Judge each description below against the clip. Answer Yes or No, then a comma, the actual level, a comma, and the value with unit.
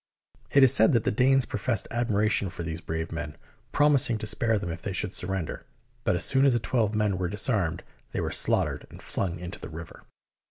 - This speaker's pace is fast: Yes, fast, 210 wpm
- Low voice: Yes, low, 105 Hz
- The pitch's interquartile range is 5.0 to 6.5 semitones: Yes, average, 5.3 semitones